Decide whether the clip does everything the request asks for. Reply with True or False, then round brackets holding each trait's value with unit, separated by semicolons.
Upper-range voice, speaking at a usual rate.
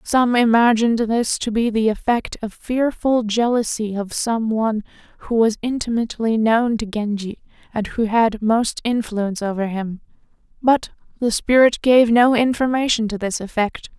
True (225 Hz; 150 wpm)